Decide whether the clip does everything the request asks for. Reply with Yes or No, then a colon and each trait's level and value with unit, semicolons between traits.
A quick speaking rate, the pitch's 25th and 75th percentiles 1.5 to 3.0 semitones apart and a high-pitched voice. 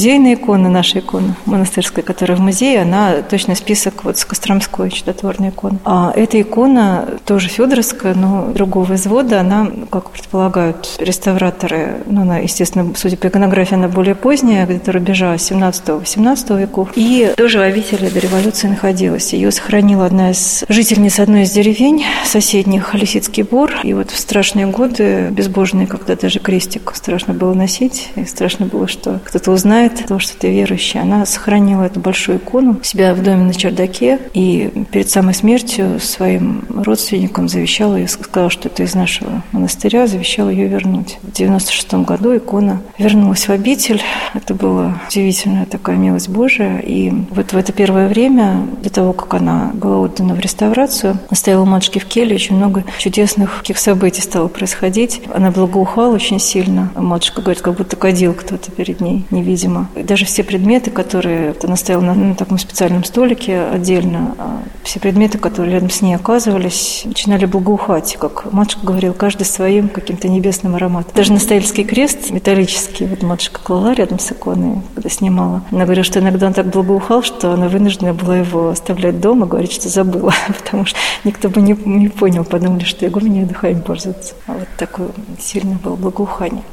Yes: fast, 165 wpm; narrow, 2.4 semitones; high, 195 Hz